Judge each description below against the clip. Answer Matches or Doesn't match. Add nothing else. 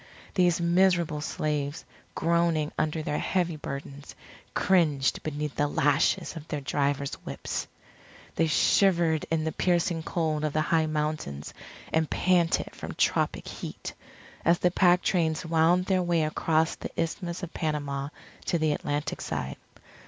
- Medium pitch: Matches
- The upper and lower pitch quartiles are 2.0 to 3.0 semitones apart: Matches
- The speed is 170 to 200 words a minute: Doesn't match